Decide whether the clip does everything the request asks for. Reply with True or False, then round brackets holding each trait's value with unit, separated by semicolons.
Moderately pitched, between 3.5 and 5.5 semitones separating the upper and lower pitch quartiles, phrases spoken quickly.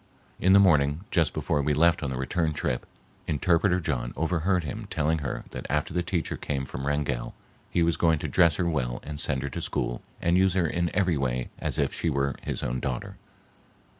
False (75 Hz; 3.9 semitones; 210 wpm)